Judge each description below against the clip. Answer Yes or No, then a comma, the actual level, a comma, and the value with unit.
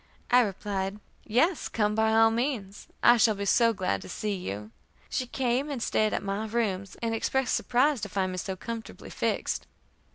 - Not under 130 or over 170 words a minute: No, average, 185 wpm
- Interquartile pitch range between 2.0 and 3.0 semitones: No, average, 3.5 semitones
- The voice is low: No, high, 220 Hz